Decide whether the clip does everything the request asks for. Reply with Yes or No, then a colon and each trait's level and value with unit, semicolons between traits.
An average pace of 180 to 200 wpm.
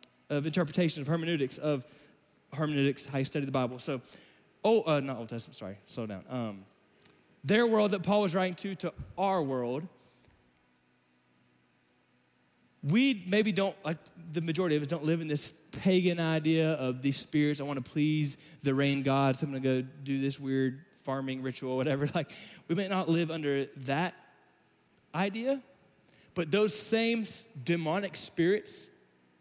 No: average, 160 wpm